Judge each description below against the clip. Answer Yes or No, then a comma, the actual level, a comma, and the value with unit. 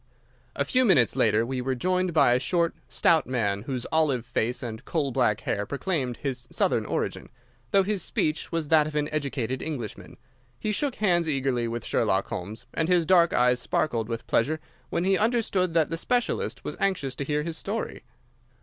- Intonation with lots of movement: Yes, wide, 5.8 semitones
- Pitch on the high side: No, medium, 150 Hz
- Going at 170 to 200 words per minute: Yes, average, 185 wpm